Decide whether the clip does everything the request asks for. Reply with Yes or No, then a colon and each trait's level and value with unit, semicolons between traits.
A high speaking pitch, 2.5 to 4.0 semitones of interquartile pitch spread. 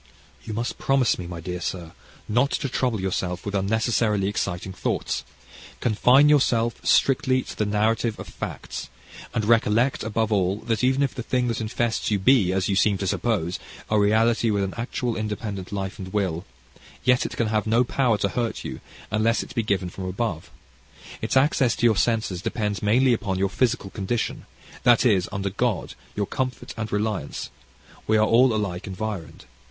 No: low, 110 Hz; average, 3.4 semitones